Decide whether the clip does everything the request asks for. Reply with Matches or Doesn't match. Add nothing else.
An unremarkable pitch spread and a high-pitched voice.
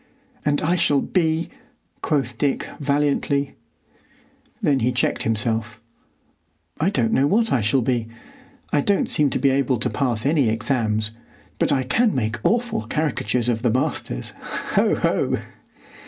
Doesn't match